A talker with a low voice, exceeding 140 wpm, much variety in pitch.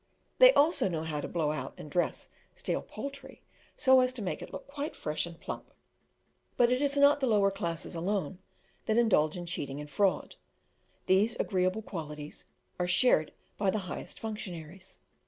No: high, 190 Hz; average, 175 wpm; wide, 6.8 semitones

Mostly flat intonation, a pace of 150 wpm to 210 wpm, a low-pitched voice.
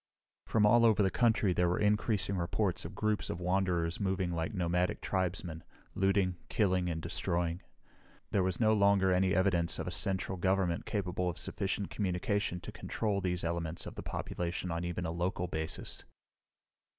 Yes: narrow, 2.2 semitones; average, 165 wpm; very low, 90 Hz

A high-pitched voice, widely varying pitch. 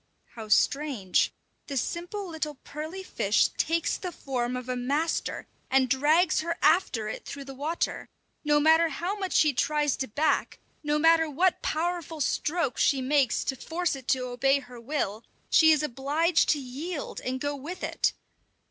No: very high, 295 Hz; average, 3.9 semitones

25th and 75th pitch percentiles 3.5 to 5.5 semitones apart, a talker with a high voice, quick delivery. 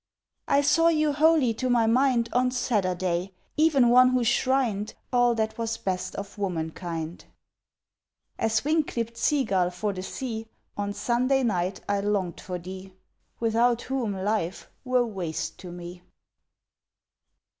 No: average, 5.2 semitones; high, 225 Hz; slow, 135 wpm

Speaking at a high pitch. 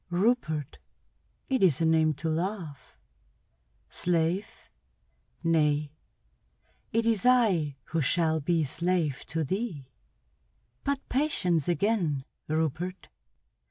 No: medium, 165 Hz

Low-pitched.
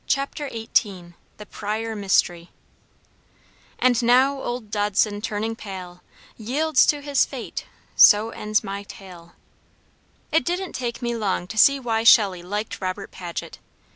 No: high, 215 Hz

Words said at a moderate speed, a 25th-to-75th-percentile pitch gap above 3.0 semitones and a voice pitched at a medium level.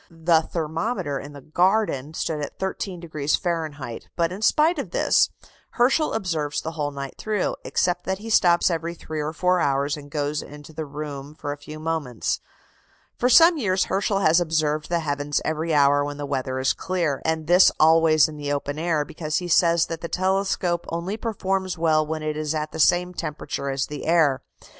Yes: average, 190 wpm; average, 3.4 semitones; medium, 160 Hz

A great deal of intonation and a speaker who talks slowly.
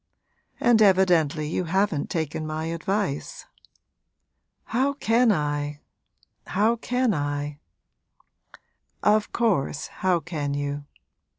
Yes: wide, 6.3 semitones; slow, 95 wpm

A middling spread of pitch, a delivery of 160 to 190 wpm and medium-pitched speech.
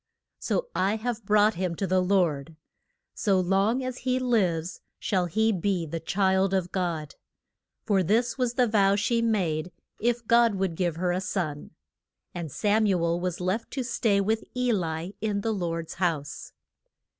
No: average, 4.2 semitones; average, 170 wpm; high, 195 Hz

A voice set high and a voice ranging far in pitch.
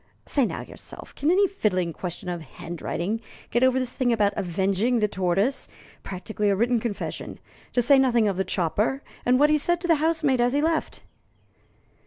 Yes: high, 235 Hz; wide, 6.0 semitones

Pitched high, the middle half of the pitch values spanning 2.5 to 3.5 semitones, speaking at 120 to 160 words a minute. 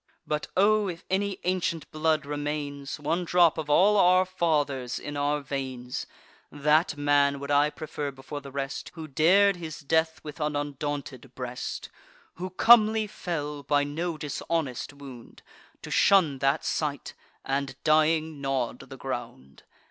No: medium, 150 Hz; average, 2.9 semitones; average, 145 wpm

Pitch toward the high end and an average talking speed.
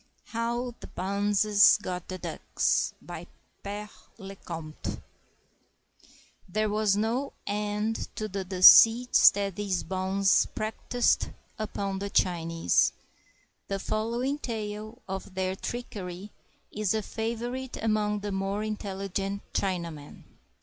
No: high, 205 Hz; slow, 110 wpm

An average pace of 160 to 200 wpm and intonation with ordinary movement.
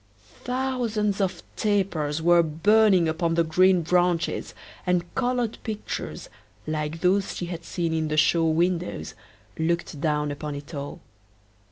No: slow, 135 wpm; average, 3.7 semitones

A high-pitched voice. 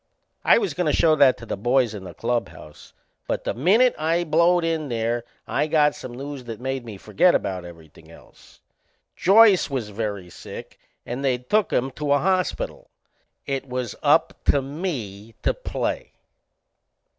No: low, 135 Hz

